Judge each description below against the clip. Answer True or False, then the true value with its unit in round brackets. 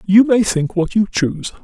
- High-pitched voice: True (195 Hz)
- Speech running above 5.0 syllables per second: True (5.2 syllables/s)